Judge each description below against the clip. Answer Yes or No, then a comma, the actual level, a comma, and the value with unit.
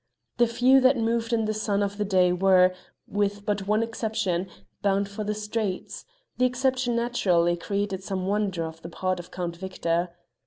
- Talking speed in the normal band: Yes, average, 180 wpm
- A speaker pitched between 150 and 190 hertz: No, high, 205 Hz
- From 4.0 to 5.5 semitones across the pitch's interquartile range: No, average, 3.5 semitones